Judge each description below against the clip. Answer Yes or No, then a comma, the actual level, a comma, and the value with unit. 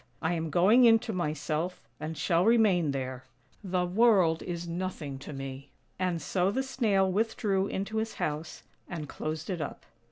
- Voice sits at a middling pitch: Yes, medium, 180 Hz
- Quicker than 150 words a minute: Yes, average, 160 wpm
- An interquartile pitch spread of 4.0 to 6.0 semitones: Yes, average, 4.5 semitones